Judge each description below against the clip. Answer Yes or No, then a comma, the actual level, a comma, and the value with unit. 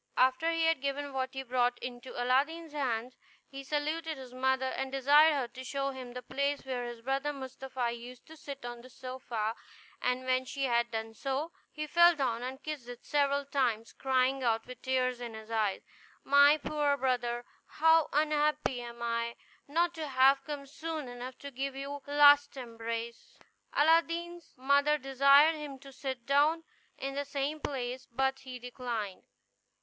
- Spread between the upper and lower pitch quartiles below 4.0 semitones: Yes, average, 2.7 semitones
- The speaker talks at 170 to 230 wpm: Yes, average, 175 wpm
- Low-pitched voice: No, very high, 265 Hz